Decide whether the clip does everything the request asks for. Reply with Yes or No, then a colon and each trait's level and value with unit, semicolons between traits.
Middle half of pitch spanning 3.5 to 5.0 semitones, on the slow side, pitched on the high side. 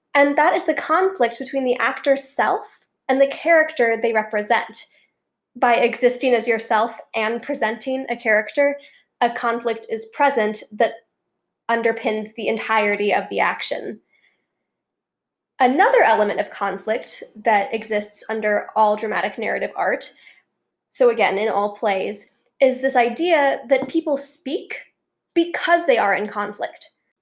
Yes: average, 4.3 semitones; slow, 130 wpm; high, 235 Hz